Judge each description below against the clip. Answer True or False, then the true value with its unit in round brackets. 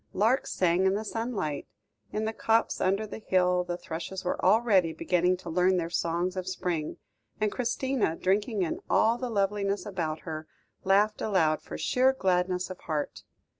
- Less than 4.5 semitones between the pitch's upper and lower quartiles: True (3.4 semitones)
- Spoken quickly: False (170 wpm)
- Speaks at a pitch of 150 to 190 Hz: True (185 Hz)